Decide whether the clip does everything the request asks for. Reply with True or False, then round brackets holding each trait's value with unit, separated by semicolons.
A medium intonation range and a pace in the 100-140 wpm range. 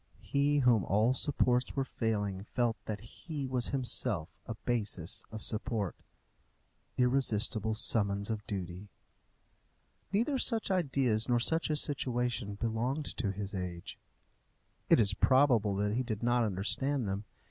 True (4.3 semitones; 135 wpm)